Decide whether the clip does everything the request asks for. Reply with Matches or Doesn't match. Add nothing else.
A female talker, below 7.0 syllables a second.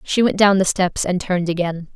Matches